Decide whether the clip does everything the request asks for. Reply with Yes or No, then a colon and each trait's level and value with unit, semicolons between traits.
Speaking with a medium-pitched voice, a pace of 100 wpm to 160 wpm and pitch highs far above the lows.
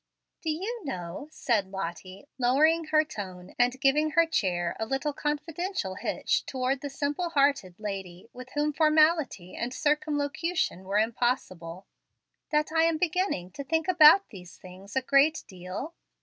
No: very high, 275 Hz; average, 150 wpm; wide, 8.2 semitones